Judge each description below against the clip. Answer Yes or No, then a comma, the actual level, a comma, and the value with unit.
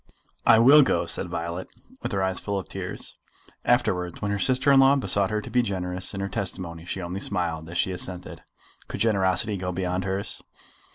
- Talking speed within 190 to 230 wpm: Yes, average, 195 wpm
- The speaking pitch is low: Yes, very low, 95 Hz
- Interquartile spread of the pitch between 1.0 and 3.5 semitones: Yes, average, 2.9 semitones